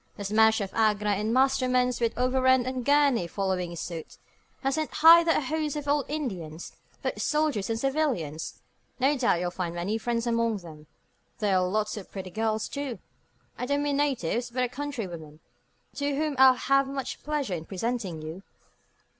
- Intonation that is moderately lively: No, wide, 6.3 semitones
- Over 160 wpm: Yes, average, 170 wpm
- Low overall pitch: No, high, 235 Hz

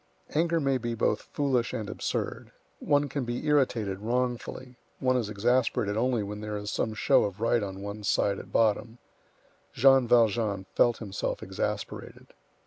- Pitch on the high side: No, low, 115 Hz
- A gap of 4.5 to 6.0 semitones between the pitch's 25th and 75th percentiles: No, average, 3.6 semitones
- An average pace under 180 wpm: Yes, average, 155 wpm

